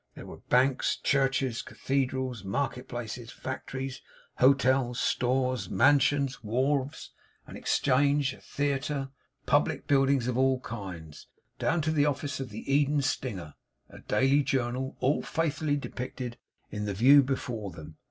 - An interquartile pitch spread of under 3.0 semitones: Yes, narrow, 2.6 semitones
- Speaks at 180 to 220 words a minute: No, slow, 135 wpm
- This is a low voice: Yes, low, 130 Hz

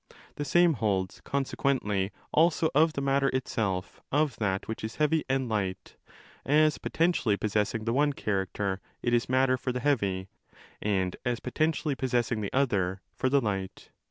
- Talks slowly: No, average, 155 wpm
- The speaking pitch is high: No, low, 125 Hz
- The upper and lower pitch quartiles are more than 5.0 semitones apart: Yes, wide, 5.6 semitones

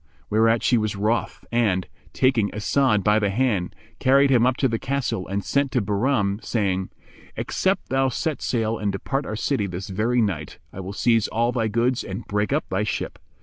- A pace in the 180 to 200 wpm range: Yes, average, 190 wpm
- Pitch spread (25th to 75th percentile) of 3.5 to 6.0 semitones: Yes, average, 4.0 semitones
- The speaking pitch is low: Yes, low, 110 Hz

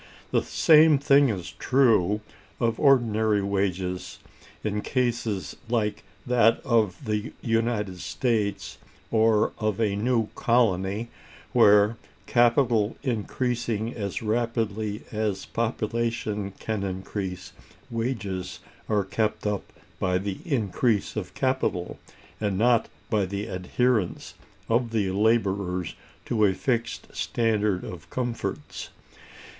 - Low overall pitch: Yes, low, 110 Hz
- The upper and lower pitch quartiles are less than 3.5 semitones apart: Yes, average, 2.8 semitones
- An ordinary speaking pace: No, slow, 105 wpm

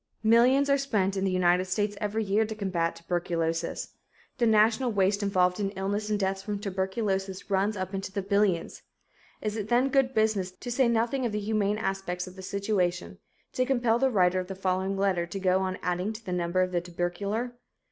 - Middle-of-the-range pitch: No, high, 195 Hz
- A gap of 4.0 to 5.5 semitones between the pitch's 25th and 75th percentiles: No, average, 2.9 semitones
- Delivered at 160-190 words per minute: No, average, 200 wpm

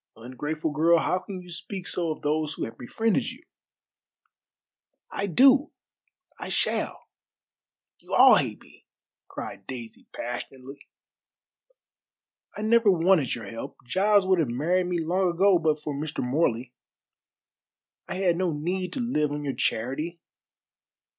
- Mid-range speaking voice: Yes, medium, 165 Hz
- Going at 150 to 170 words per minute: No, average, 140 wpm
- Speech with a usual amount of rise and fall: Yes, average, 4.7 semitones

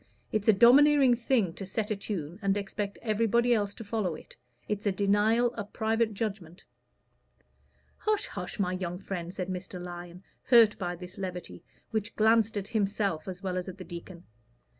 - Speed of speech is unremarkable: Yes, average, 175 wpm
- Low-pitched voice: No, high, 200 Hz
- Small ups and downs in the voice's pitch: No, average, 3.4 semitones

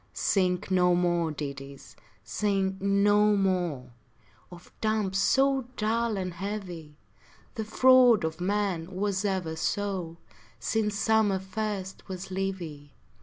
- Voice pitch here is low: No, high, 190 Hz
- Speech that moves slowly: Yes, slow, 115 wpm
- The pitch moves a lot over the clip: No, average, 3.3 semitones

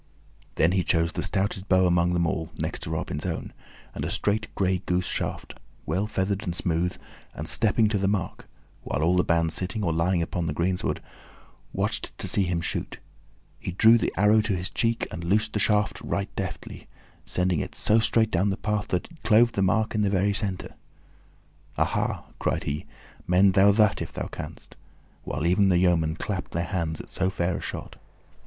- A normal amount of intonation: Yes, average, 3.1 semitones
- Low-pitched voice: Yes, very low, 95 Hz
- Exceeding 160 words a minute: Yes, average, 195 wpm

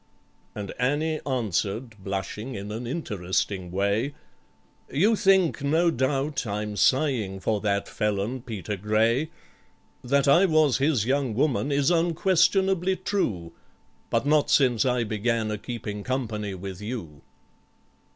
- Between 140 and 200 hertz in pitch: No, low, 120 Hz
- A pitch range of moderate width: No, wide, 5.8 semitones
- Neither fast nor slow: No, slow, 125 wpm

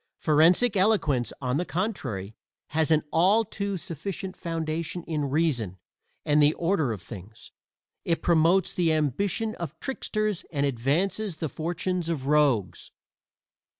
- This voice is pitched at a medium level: Yes, medium, 160 Hz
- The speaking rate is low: Yes, slow, 130 wpm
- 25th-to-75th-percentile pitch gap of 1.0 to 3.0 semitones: No, average, 4.5 semitones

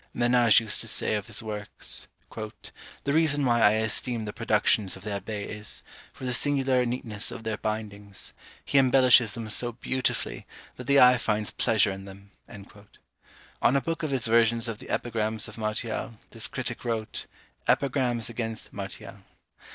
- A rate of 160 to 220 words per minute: Yes, average, 165 wpm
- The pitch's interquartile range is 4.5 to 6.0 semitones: No, average, 2.8 semitones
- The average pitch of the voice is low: Yes, low, 115 Hz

